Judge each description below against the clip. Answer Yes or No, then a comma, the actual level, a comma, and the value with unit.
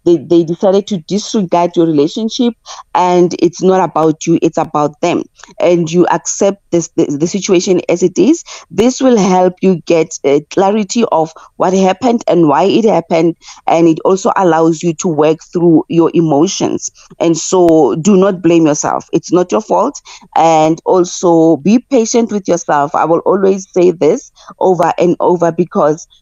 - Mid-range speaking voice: Yes, medium, 175 Hz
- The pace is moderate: Yes, average, 170 wpm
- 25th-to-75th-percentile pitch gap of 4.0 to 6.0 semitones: No, average, 2.9 semitones